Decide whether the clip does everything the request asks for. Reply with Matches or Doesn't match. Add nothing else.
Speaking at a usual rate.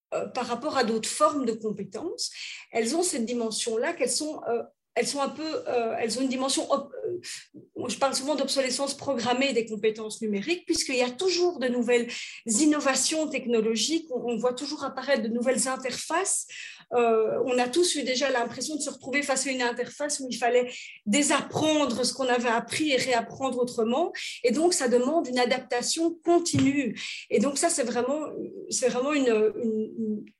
Matches